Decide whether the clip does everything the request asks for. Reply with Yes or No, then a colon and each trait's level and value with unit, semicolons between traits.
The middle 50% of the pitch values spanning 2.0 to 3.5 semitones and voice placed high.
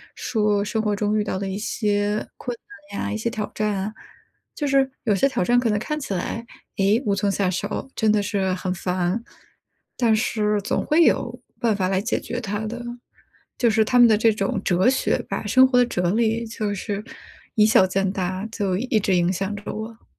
Yes: average, 3.0 semitones; high, 210 Hz